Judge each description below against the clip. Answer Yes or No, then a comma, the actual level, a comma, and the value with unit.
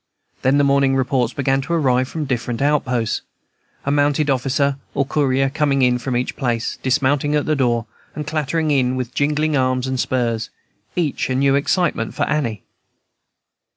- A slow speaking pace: No, average, 170 wpm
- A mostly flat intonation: Yes, narrow, 2.3 semitones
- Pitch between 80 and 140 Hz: Yes, low, 135 Hz